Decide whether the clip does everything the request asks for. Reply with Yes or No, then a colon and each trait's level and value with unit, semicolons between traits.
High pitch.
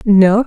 Yes: high, 205 Hz